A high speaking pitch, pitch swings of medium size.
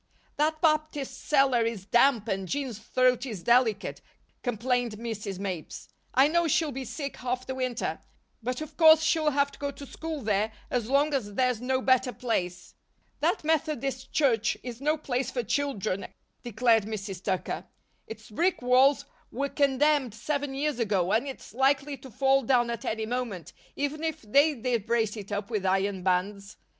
Yes: very high, 250 Hz; average, 4.4 semitones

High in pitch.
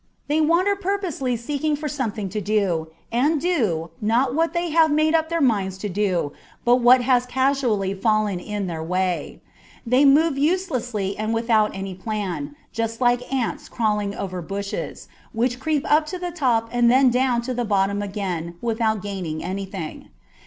Yes: high, 230 Hz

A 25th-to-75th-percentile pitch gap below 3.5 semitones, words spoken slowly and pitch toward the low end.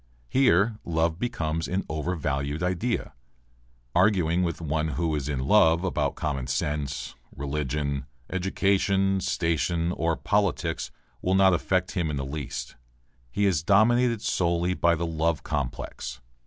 No: average, 4.1 semitones; slow, 130 wpm; very low, 85 Hz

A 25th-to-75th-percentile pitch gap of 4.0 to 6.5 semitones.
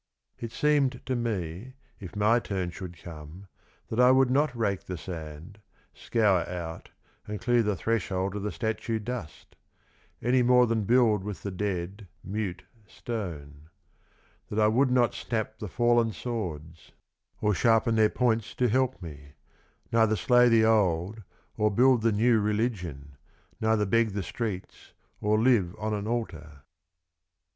Yes: average, 4.3 semitones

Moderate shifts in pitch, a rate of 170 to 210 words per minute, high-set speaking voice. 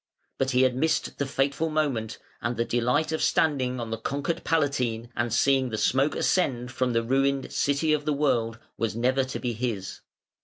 No: average, 3.2 semitones; average, 190 wpm; low, 130 Hz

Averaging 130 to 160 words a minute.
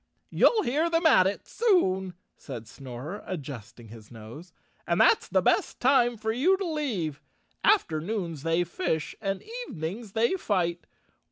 Yes: average, 145 wpm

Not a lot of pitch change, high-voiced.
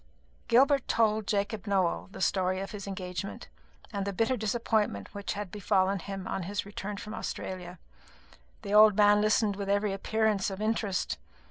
Yes: narrow, 1.8 semitones; high, 200 Hz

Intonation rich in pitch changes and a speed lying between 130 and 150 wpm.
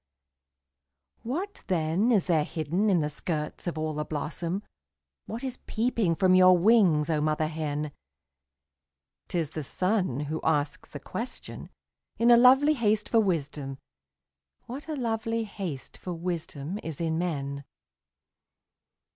Yes: wide, 6.4 semitones; average, 140 wpm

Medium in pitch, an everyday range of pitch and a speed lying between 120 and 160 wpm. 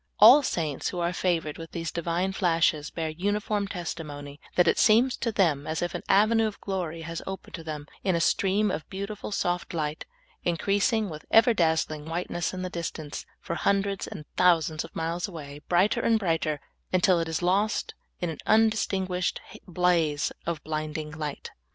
No: medium, 175 Hz; average, 3.7 semitones; average, 175 wpm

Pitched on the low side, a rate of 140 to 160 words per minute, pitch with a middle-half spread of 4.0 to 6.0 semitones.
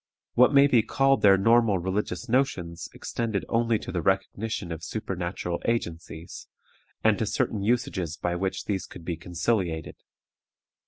Yes: very low, 95 Hz; average, 145 wpm; average, 5.0 semitones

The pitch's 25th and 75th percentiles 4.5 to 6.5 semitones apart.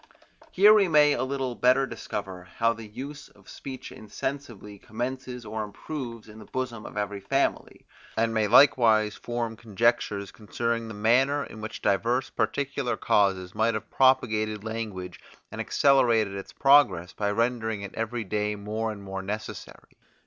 No: average, 3.5 semitones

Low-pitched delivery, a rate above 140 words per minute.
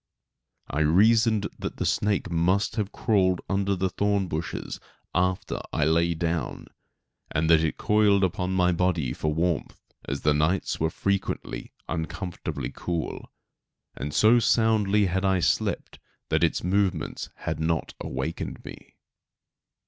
No: very low, 90 Hz; slow, 135 wpm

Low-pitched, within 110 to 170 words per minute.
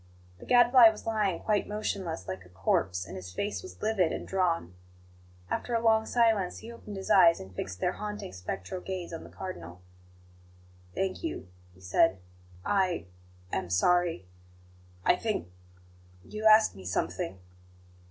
No: medium, 180 Hz; average, 150 wpm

